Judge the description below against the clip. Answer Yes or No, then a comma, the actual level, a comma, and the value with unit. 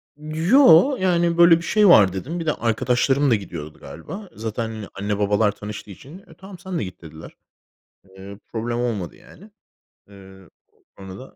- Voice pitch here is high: No, low, 115 Hz